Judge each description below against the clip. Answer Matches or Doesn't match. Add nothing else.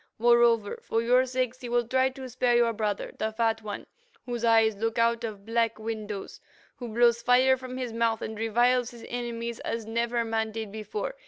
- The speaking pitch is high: Matches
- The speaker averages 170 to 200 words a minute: Matches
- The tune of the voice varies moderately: Doesn't match